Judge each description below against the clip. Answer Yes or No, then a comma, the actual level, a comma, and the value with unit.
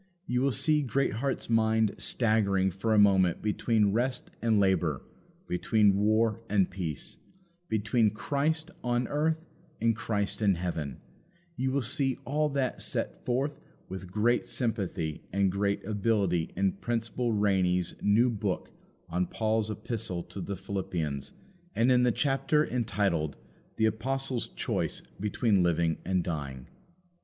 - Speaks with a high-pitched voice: No, low, 110 Hz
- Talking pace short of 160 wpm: Yes, slow, 135 wpm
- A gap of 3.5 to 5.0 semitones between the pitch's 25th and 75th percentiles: Yes, average, 4.3 semitones